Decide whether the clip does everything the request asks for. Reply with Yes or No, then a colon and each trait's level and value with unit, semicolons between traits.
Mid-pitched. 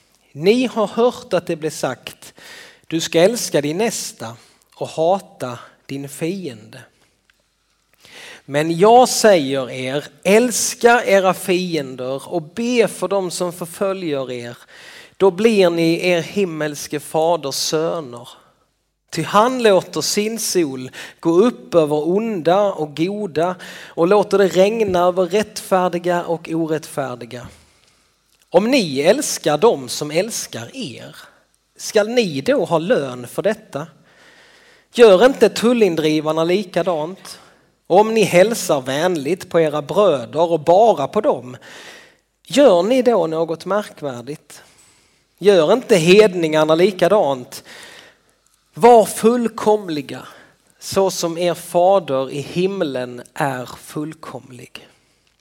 Yes: medium, 175 Hz